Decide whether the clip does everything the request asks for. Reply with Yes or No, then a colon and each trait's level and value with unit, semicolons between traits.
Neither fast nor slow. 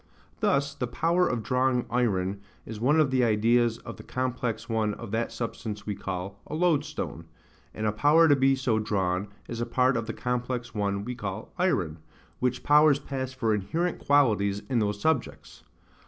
Yes: average, 180 wpm